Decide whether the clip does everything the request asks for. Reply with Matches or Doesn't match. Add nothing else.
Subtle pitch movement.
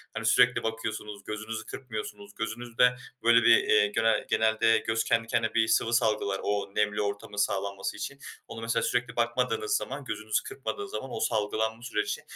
Matches